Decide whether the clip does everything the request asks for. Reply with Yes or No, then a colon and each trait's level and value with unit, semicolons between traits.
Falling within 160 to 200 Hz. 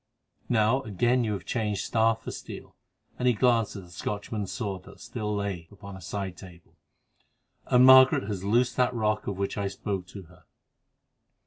No: low, 105 Hz